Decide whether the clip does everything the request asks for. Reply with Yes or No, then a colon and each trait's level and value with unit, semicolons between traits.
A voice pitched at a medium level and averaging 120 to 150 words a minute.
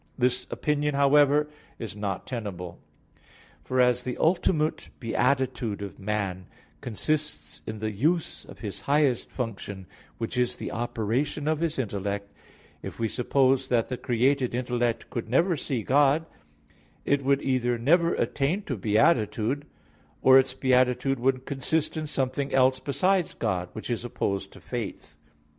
No: low, 130 Hz; average, 145 wpm